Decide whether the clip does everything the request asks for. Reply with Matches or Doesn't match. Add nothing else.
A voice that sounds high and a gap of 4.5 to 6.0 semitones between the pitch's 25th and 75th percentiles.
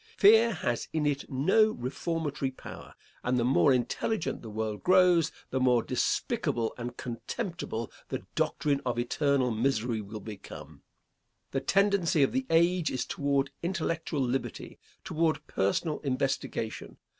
Doesn't match